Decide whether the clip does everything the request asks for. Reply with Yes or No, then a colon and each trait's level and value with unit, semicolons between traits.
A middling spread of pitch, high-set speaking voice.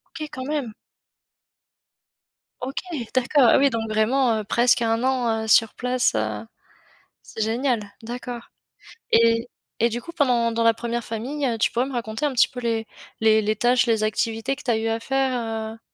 No: narrow, 2.3 semitones; high, 235 Hz